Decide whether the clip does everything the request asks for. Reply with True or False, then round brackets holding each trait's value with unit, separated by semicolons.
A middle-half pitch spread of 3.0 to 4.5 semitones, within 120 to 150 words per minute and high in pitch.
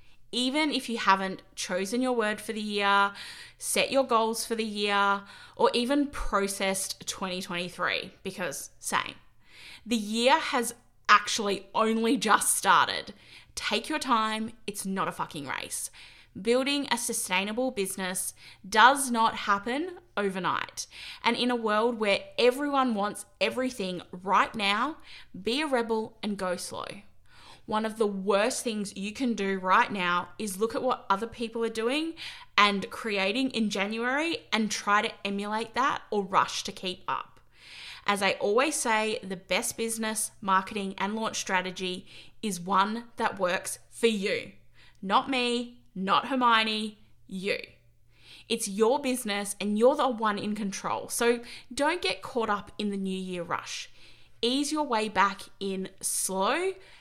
True (3.6 semitones; 145 wpm; 215 Hz)